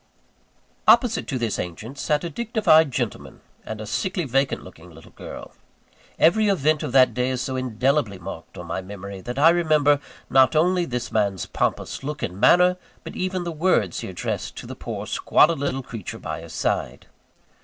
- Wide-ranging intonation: Yes, wide, 7.4 semitones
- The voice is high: No, low, 135 Hz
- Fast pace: No, average, 180 wpm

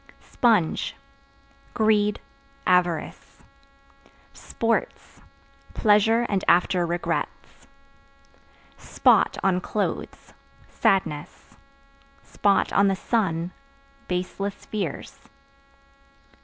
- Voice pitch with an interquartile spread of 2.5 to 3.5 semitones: Yes, average, 3.0 semitones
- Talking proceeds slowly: Yes, slow, 60 wpm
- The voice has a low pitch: No, high, 195 Hz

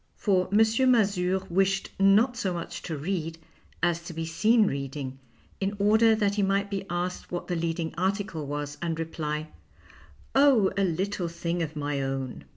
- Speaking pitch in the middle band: Yes, medium, 180 Hz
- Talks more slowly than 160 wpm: No, average, 170 wpm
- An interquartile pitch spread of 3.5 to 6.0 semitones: Yes, average, 3.8 semitones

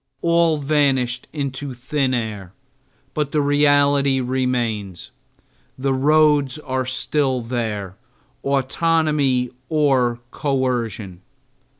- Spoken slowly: Yes, slow, 85 wpm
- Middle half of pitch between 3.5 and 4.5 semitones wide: No, average, 2.9 semitones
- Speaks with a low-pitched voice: Yes, low, 130 Hz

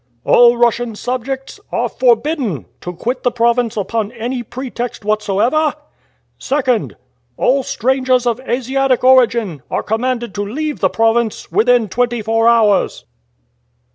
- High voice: Yes, high, 240 Hz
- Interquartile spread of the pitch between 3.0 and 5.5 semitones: No, narrow, 2.5 semitones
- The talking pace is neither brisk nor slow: No, slow, 125 wpm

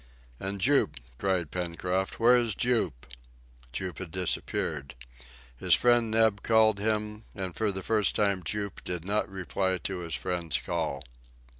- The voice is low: Yes, very low, 95 Hz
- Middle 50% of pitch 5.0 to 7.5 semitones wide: No, average, 3.4 semitones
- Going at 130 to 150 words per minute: Yes, average, 145 wpm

